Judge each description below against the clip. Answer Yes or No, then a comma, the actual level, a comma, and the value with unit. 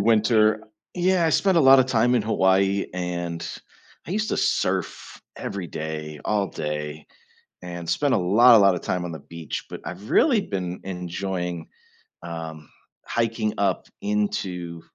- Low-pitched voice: Yes, very low, 95 Hz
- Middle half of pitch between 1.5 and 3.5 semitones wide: No, average, 5.3 semitones